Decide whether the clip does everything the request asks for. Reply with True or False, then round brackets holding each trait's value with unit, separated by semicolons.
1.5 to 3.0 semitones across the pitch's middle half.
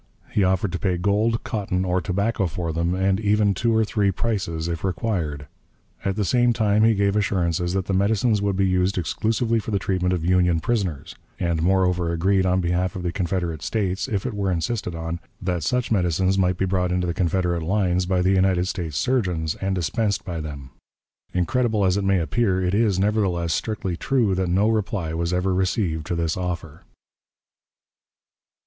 True (2.7 semitones)